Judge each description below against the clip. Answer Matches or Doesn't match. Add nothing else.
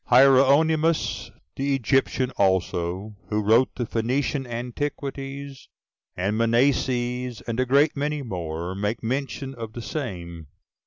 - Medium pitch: Doesn't match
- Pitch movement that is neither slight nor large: Matches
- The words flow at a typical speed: Doesn't match